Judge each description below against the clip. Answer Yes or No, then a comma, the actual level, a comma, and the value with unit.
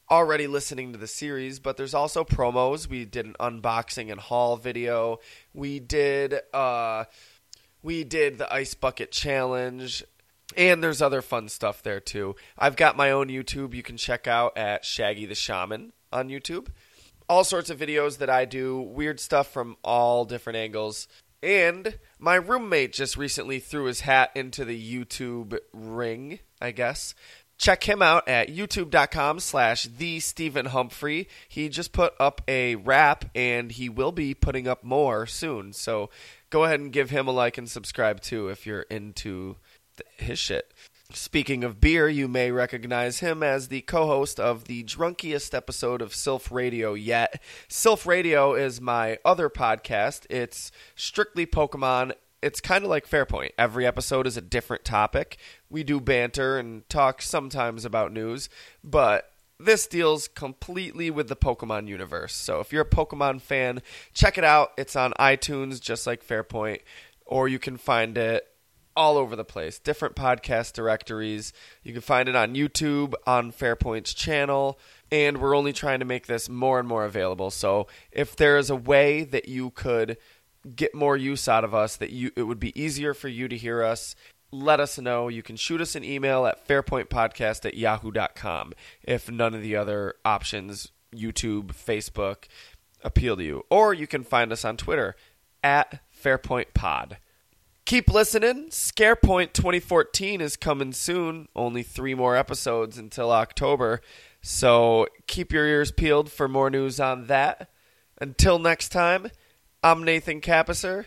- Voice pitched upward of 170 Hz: No, low, 130 Hz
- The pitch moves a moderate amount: Yes, average, 3.9 semitones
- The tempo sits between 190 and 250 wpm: No, average, 165 wpm